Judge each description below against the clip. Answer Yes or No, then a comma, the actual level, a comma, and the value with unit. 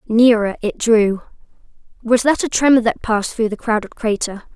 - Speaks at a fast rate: No, average, 170 wpm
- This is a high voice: Yes, high, 225 Hz